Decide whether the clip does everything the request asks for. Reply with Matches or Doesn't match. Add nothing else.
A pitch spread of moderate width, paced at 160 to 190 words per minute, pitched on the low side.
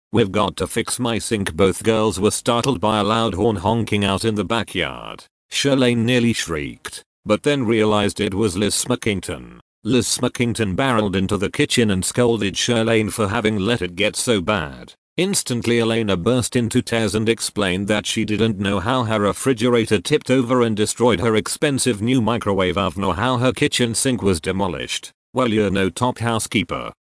Matches